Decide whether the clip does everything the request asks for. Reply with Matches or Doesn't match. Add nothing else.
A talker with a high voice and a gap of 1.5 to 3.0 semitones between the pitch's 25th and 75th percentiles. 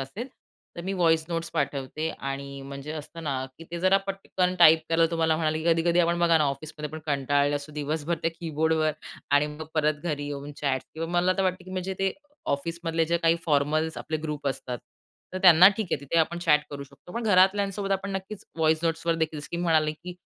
Doesn't match